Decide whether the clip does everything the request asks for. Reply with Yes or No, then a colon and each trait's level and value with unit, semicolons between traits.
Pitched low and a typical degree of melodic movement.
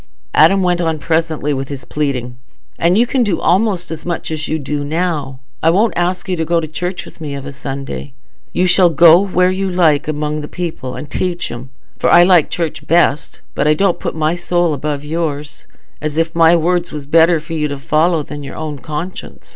No: medium, 160 Hz; average, 3.0 semitones